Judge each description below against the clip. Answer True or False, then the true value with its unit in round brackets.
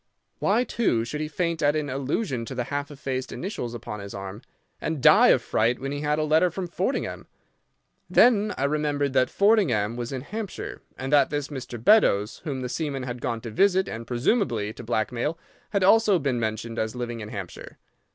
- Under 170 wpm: False (195 wpm)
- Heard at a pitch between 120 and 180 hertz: True (135 Hz)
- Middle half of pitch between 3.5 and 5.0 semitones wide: False (5.5 semitones)